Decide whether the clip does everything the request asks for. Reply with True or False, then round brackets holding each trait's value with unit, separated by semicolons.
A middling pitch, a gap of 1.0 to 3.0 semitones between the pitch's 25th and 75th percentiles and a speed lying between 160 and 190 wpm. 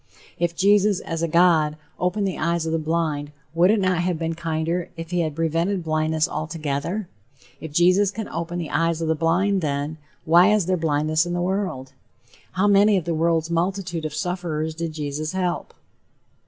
True (165 Hz; 2.4 semitones; 185 wpm)